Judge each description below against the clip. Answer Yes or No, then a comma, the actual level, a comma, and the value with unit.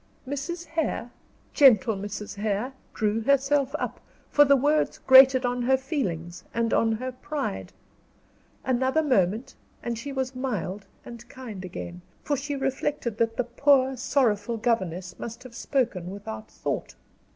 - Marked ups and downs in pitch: No, average, 4.5 semitones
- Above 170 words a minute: No, average, 140 wpm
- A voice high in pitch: Yes, high, 245 Hz